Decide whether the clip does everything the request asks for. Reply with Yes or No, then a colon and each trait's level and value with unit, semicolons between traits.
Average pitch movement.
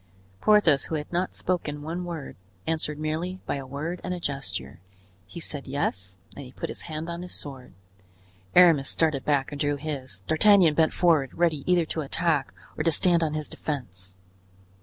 Yes: average, 3.6 semitones